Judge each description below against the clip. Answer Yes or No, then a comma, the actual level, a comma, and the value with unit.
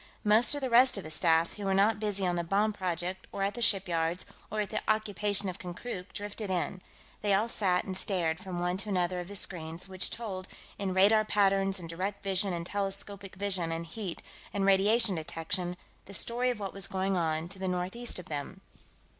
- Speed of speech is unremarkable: No, fast, 210 wpm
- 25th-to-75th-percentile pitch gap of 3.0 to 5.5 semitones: No, narrow, 2.5 semitones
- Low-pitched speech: No, high, 195 Hz